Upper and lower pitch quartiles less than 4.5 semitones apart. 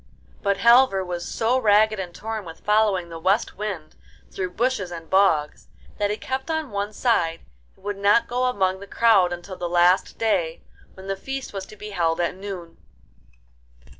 Yes: average, 3.6 semitones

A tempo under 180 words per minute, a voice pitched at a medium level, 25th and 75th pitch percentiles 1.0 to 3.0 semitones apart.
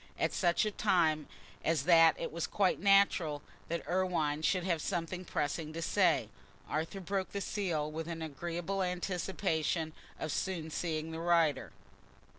Yes: average, 150 wpm; medium, 170 Hz; average, 2.7 semitones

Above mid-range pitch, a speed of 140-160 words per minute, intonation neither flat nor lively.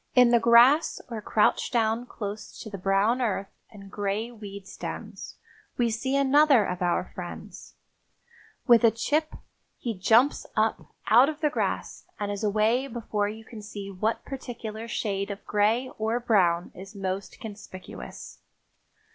Yes: high, 220 Hz; average, 150 wpm; average, 3.0 semitones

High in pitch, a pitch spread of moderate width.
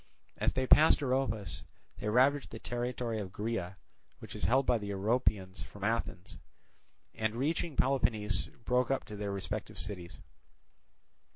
No: low, 115 Hz; average, 3.9 semitones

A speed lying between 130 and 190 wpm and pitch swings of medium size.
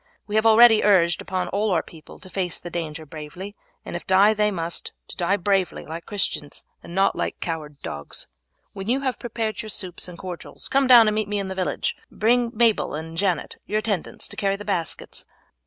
No: fast, 205 wpm; average, 3.9 semitones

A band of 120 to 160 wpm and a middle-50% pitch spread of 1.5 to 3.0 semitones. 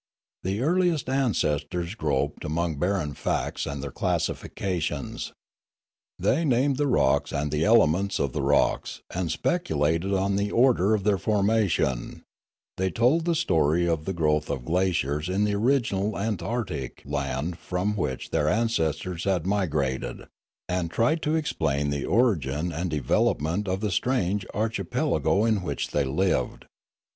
No: average, 145 wpm; wide, 6.2 semitones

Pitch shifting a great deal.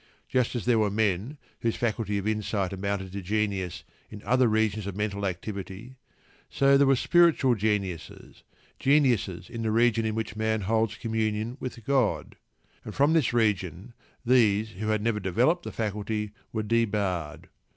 No: average, 2.8 semitones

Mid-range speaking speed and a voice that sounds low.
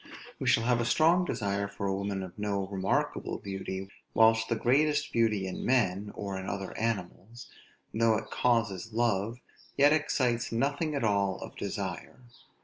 Yes: average, 160 wpm; low, 110 Hz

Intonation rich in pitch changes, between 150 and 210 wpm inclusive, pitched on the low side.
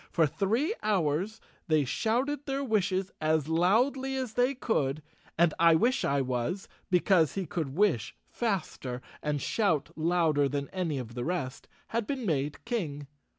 No: wide, 7.2 semitones; average, 155 wpm; medium, 175 Hz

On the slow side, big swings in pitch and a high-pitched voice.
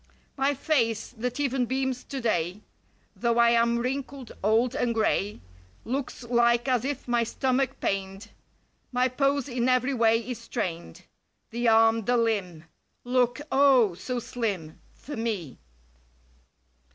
No: slow, 130 wpm; narrow, 2.5 semitones; high, 235 Hz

